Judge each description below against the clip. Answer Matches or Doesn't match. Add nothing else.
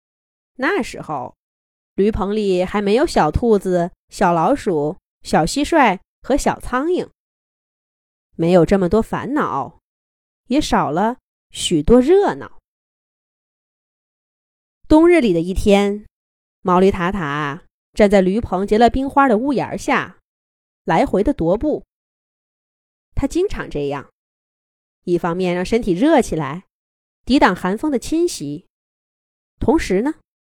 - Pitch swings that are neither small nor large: Doesn't match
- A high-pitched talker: Matches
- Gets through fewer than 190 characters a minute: Matches